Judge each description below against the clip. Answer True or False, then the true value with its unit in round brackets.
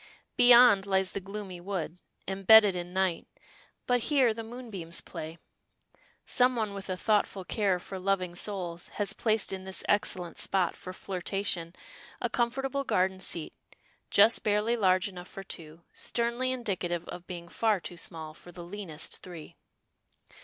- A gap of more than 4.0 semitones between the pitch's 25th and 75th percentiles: False (3.5 semitones)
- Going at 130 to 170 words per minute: True (150 wpm)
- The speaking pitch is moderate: False (195 Hz)